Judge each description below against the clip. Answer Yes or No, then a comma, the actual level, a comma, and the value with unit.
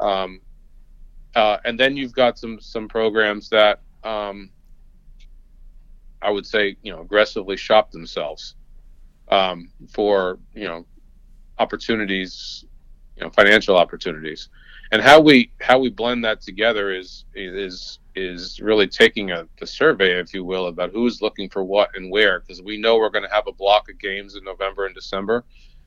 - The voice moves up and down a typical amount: Yes, average, 3.5 semitones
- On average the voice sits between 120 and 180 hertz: No, low, 100 Hz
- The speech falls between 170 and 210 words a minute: No, average, 160 wpm